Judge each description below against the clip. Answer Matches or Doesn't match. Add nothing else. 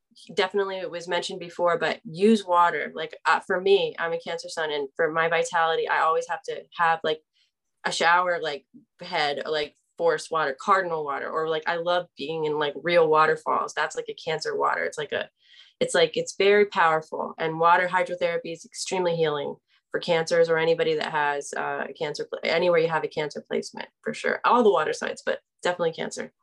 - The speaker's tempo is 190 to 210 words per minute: Matches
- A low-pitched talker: Doesn't match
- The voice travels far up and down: Matches